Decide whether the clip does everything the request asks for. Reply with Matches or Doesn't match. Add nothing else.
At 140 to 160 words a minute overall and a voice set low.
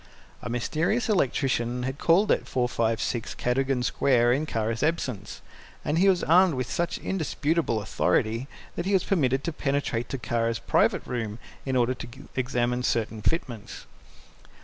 Matches